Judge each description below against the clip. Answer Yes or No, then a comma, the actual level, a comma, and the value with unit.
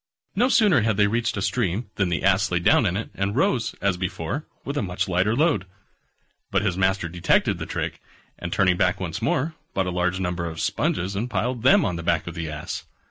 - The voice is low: Yes, very low, 95 Hz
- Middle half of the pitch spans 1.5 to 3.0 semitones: No, average, 4.1 semitones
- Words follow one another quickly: Yes, fast, 225 wpm